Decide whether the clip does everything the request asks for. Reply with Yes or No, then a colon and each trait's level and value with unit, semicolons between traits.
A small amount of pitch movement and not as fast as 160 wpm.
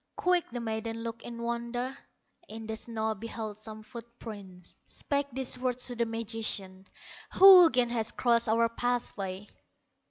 Yes: narrow, 1.8 semitones; average, 150 wpm